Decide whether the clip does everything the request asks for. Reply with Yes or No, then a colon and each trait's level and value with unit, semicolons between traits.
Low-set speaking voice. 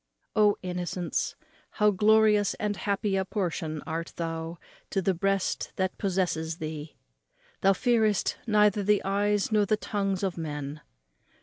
No: high, 195 Hz